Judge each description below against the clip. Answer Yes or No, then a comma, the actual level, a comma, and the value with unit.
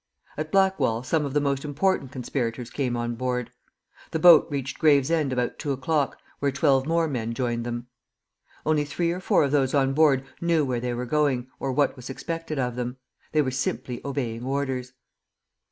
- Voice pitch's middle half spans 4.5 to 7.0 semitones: No, average, 3.3 semitones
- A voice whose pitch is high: No, low, 135 Hz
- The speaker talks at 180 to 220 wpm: Yes, average, 185 wpm